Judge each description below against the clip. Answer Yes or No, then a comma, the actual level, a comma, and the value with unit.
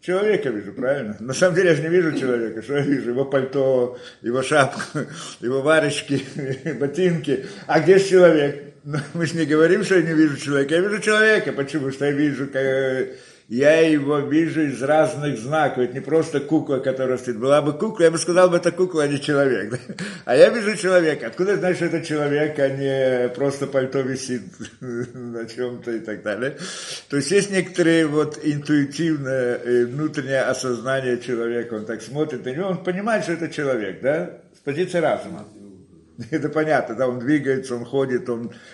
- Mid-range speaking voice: Yes, medium, 145 Hz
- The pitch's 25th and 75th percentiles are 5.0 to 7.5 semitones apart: No, average, 3.6 semitones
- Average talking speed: No, fast, 180 wpm